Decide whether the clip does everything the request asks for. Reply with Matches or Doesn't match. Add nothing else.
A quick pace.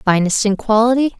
Doesn't match